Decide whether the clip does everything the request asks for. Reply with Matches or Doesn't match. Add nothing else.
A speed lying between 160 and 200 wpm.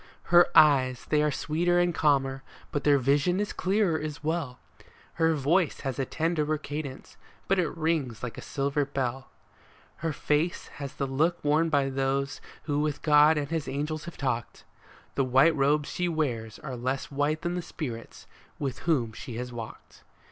Matches